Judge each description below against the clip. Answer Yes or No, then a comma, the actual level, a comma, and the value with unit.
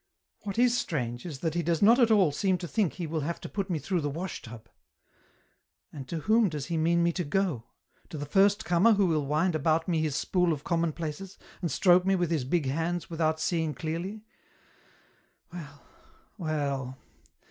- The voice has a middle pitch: Yes, medium, 165 Hz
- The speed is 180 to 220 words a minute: Yes, average, 200 wpm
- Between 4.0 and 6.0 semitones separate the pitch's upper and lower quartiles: No, average, 3.6 semitones